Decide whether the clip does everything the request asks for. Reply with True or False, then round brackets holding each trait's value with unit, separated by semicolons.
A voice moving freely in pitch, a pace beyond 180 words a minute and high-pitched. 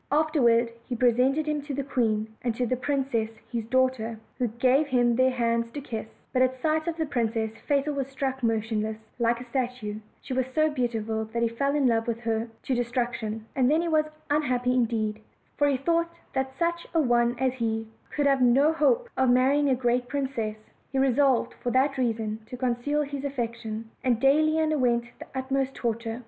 False (3.2 semitones; 195 wpm; 255 Hz)